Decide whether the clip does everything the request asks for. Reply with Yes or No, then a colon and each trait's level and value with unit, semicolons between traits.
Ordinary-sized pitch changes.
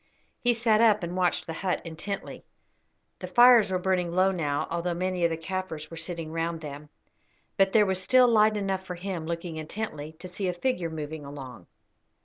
Yes: average, 3.2 semitones